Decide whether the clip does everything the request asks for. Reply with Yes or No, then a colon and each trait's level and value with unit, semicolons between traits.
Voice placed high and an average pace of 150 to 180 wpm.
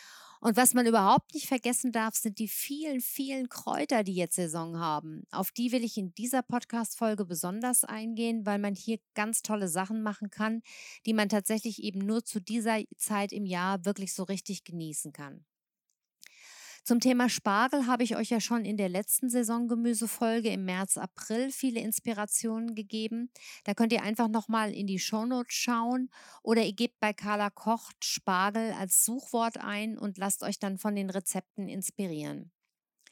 Yes: high, 220 Hz; average, 170 wpm